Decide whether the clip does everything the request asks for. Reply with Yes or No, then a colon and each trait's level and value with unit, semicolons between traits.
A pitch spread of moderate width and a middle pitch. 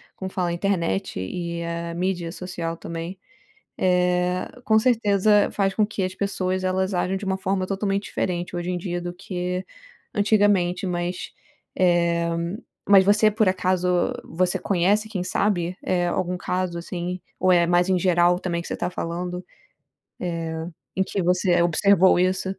No: narrow, 1.7 semitones; medium, 180 Hz